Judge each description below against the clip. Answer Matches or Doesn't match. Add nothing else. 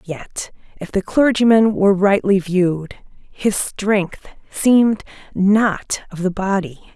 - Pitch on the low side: Doesn't match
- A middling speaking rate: Doesn't match